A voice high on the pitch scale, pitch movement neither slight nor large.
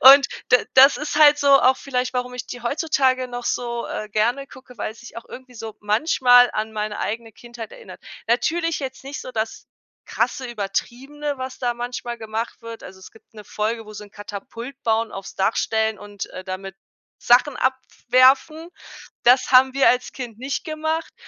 Yes: high, 245 Hz; average, 3.3 semitones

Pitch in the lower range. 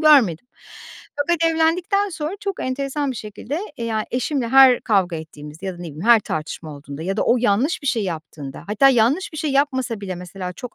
No: high, 235 Hz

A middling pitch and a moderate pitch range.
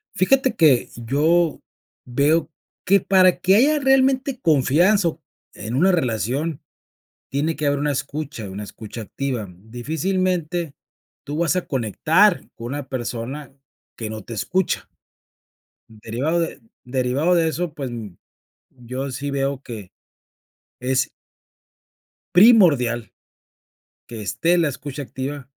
No: medium, 145 Hz; wide, 5.8 semitones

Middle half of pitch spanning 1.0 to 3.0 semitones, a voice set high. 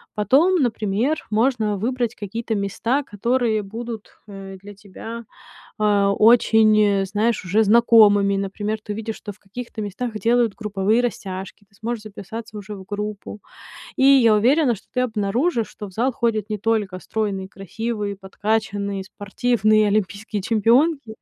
Yes: narrow, 2.5 semitones; high, 215 Hz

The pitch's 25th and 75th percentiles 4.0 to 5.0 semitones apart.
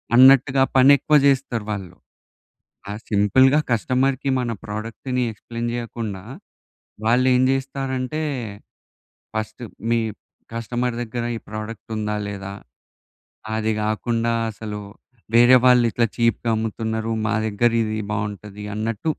No: average, 2.9 semitones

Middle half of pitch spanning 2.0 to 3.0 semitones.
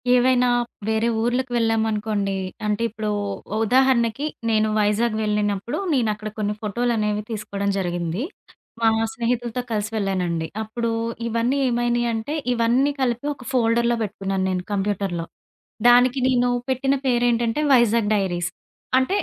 Yes: average, 2.7 semitones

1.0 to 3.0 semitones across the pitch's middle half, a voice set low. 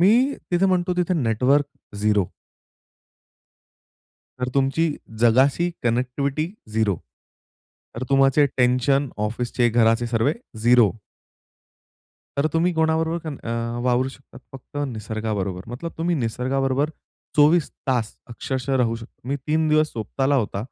No: average, 4.6 semitones; low, 130 Hz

